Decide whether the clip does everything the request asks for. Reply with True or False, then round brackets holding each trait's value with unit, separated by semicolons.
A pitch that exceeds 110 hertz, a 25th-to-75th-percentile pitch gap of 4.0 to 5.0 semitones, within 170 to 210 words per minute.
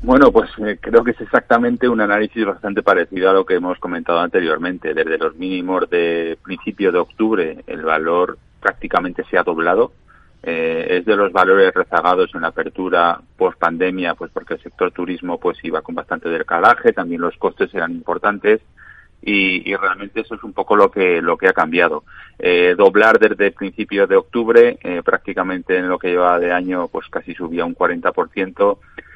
False (95 Hz; 4.3 semitones; 185 wpm)